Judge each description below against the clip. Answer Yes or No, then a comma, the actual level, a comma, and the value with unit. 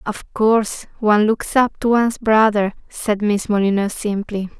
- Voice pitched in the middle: No, high, 210 Hz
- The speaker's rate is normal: Yes, average, 155 wpm